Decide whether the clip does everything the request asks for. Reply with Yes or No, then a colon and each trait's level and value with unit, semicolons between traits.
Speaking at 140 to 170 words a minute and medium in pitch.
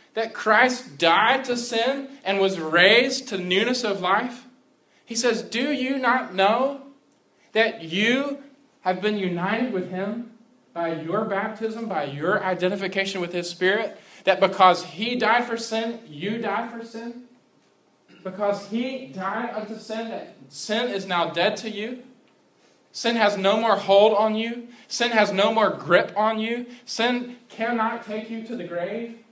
No: average, 160 wpm; high, 220 Hz